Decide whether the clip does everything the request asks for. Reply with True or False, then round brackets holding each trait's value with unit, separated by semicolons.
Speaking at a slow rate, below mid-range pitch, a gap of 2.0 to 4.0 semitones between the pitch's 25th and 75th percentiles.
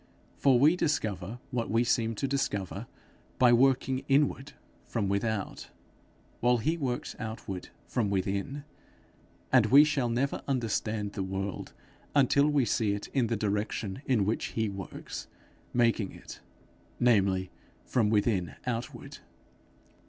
False (130 wpm; 115 Hz; 4.5 semitones)